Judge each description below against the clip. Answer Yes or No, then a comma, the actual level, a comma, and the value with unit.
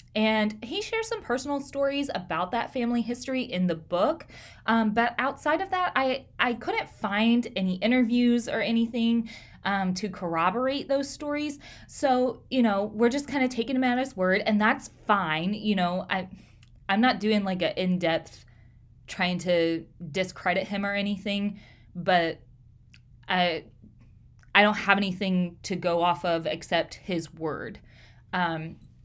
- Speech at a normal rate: Yes, average, 155 wpm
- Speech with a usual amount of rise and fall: No, wide, 6.0 semitones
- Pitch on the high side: Yes, high, 200 Hz